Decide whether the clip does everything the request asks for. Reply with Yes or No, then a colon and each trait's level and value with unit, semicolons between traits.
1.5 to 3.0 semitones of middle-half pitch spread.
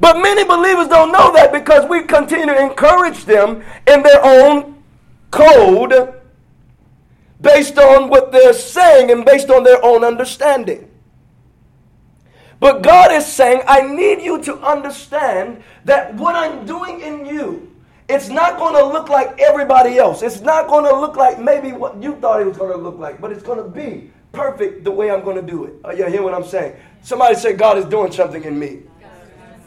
No: average, 5.0 semitones